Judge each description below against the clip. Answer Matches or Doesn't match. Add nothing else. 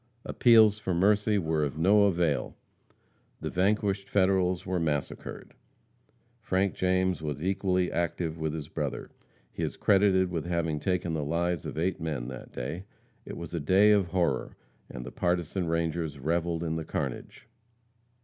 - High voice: Doesn't match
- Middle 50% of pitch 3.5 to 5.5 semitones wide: Doesn't match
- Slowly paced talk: Doesn't match